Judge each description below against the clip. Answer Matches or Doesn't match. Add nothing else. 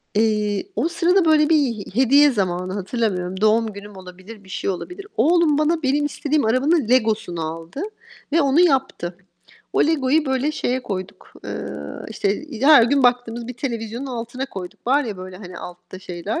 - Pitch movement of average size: Doesn't match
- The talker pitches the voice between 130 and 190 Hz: Doesn't match